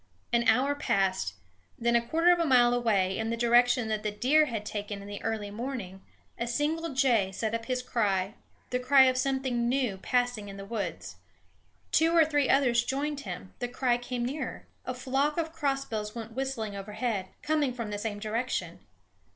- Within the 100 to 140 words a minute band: No, average, 180 wpm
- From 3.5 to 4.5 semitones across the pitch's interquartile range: Yes, average, 4.0 semitones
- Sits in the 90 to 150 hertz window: No, high, 240 Hz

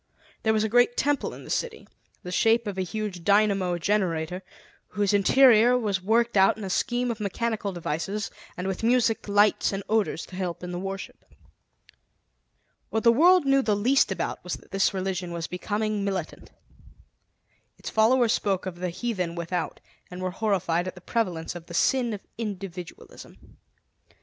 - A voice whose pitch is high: Yes, high, 200 Hz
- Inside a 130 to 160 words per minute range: No, average, 170 wpm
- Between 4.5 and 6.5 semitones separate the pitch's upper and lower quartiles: No, average, 3.8 semitones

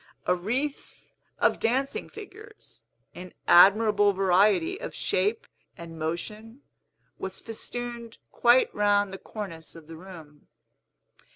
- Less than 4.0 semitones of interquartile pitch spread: No, average, 4.8 semitones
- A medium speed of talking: No, slow, 110 wpm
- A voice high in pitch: Yes, high, 205 Hz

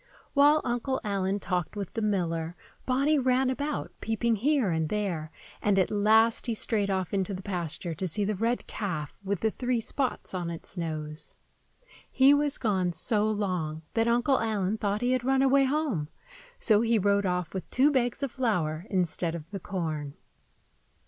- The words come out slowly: No, average, 175 wpm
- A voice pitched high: Yes, high, 205 Hz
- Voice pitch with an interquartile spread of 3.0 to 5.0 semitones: No, wide, 5.4 semitones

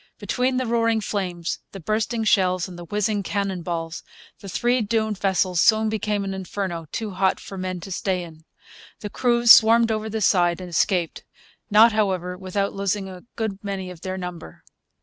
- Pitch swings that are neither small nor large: Yes, average, 3.2 semitones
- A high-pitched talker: Yes, high, 195 Hz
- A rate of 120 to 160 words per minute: No, average, 180 wpm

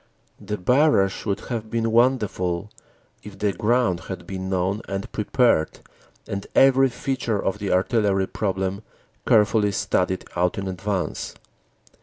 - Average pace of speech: No, slow, 130 wpm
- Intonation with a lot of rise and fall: No, average, 3.3 semitones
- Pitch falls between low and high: No, low, 100 Hz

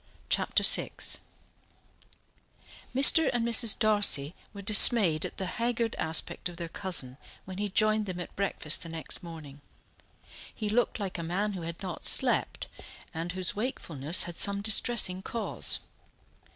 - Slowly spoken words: No, average, 145 wpm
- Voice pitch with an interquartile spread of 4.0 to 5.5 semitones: Yes, average, 4.3 semitones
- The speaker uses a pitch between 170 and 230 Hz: Yes, high, 190 Hz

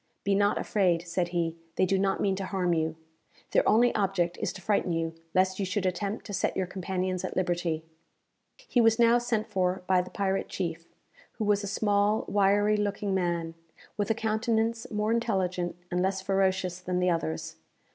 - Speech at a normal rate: Yes, average, 185 wpm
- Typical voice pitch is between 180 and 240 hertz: Yes, high, 190 Hz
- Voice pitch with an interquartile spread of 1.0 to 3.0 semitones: Yes, narrow, 2.6 semitones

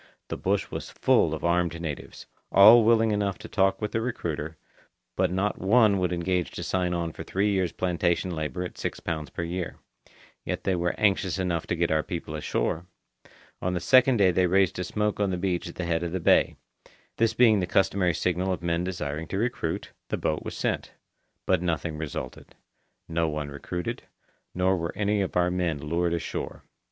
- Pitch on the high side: No, very low, 90 Hz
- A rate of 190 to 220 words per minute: Yes, average, 195 wpm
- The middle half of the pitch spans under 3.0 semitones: Yes, narrow, 2.6 semitones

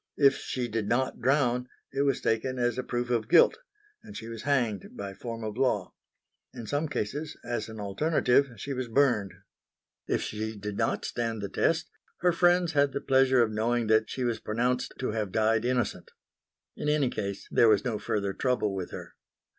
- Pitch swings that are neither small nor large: Yes, average, 3.7 semitones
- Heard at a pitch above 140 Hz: No, low, 120 Hz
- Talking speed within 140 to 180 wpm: No, average, 190 wpm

